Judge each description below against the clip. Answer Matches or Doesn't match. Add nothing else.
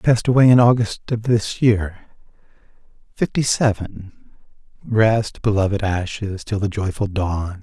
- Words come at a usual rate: Doesn't match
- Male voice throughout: Matches